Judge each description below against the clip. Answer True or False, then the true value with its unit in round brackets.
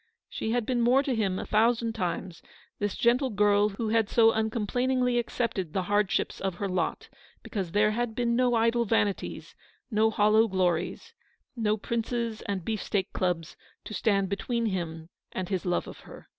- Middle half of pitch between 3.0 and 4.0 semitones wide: True (3.4 semitones)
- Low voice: False (215 Hz)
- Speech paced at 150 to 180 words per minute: True (170 wpm)